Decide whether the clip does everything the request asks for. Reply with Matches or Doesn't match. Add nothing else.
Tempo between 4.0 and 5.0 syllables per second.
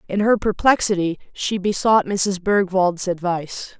Matches